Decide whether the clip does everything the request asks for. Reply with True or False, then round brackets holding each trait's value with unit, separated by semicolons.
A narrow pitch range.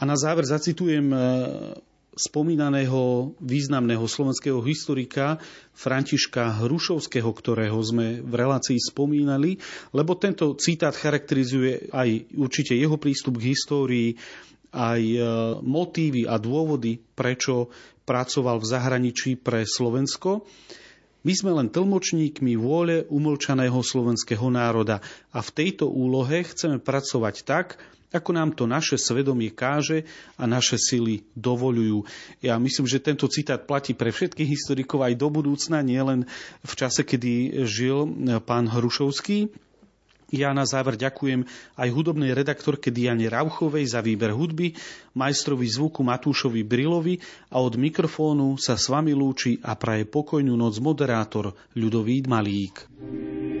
False (3.6 semitones)